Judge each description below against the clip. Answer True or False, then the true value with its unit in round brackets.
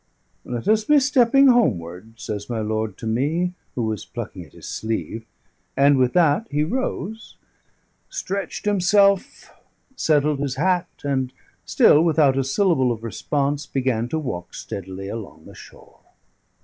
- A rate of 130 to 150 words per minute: True (145 wpm)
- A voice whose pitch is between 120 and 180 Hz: True (140 Hz)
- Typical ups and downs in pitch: False (8.1 semitones)